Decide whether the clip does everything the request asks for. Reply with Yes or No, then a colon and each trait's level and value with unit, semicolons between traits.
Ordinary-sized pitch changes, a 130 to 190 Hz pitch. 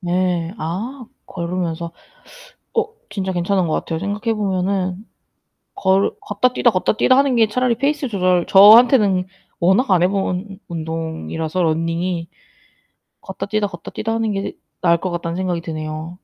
Yes: average, 3.6 semitones; medium, 185 Hz